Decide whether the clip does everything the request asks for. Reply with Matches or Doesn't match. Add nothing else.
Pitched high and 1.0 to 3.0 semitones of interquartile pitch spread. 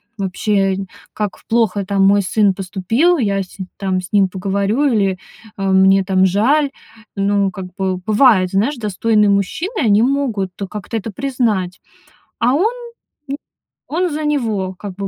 Doesn't match